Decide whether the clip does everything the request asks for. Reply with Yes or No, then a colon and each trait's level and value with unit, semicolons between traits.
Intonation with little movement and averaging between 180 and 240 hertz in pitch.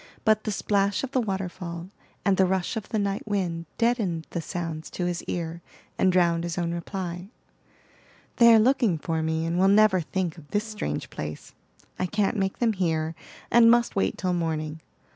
No: average, 3.6 semitones; medium, 185 Hz